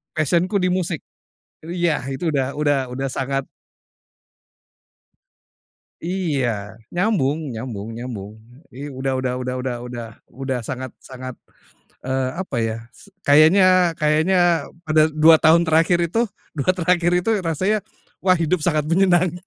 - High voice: No, medium, 155 Hz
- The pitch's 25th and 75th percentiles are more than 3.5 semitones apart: Yes, average, 5.0 semitones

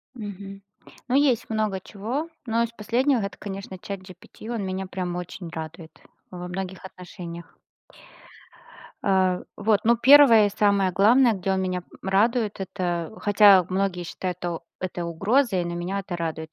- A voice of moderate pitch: No, high, 195 Hz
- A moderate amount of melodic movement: Yes, average, 3.3 semitones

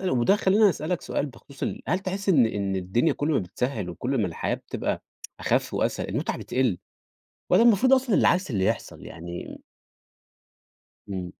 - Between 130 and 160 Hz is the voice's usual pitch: Yes, low, 135 Hz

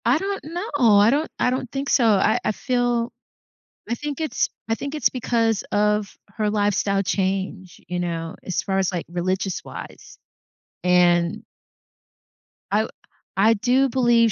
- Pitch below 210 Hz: No, high, 215 Hz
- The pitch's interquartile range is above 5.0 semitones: No, average, 4.6 semitones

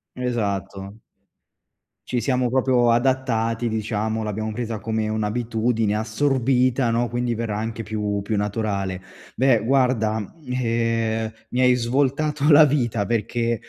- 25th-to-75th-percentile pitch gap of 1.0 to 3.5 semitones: Yes, narrow, 2.5 semitones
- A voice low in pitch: Yes, low, 115 Hz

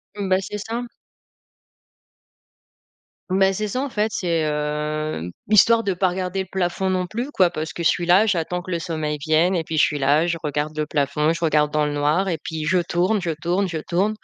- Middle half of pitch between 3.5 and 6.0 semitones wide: Yes, average, 3.9 semitones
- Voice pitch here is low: No, medium, 175 Hz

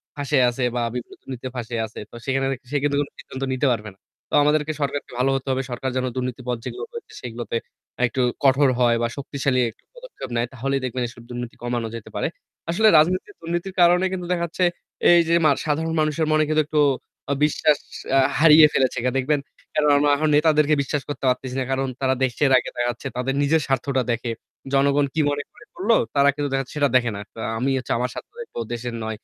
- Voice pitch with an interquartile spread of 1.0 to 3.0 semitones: No, average, 3.4 semitones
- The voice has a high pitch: No, medium, 140 Hz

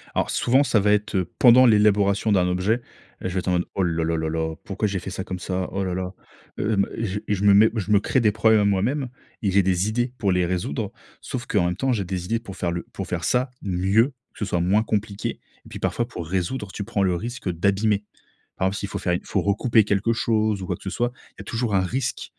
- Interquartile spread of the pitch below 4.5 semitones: Yes, average, 3.2 semitones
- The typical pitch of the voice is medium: No, low, 100 Hz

